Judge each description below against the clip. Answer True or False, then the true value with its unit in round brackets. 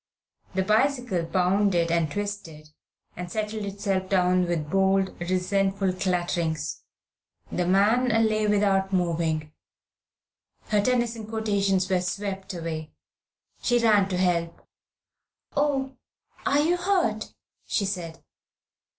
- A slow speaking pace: True (105 wpm)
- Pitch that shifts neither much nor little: True (3.3 semitones)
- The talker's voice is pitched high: True (195 Hz)